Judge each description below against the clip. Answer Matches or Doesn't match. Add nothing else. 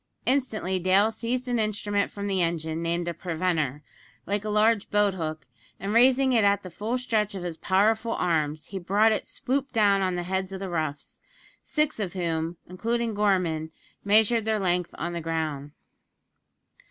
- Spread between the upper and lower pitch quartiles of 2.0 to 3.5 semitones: Doesn't match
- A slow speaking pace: Doesn't match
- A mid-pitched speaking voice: Doesn't match